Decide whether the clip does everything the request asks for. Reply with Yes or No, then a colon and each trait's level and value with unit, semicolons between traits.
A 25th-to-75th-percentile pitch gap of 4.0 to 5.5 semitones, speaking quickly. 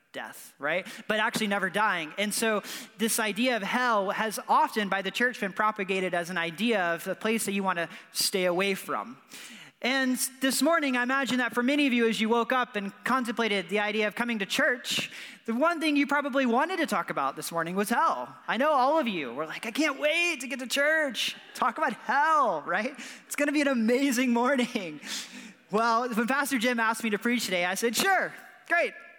Yes: average, 4.7 semitones; fast, 215 wpm